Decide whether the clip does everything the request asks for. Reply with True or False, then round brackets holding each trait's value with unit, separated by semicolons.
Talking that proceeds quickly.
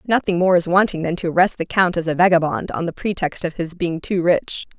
True (250 wpm)